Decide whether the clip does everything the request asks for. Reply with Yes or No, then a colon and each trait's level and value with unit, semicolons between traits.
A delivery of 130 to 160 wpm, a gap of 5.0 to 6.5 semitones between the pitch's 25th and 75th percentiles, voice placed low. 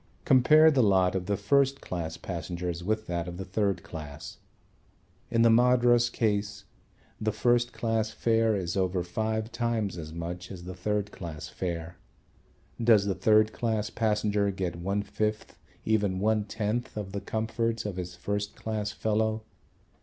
No: average, 155 wpm; average, 3.5 semitones; low, 105 Hz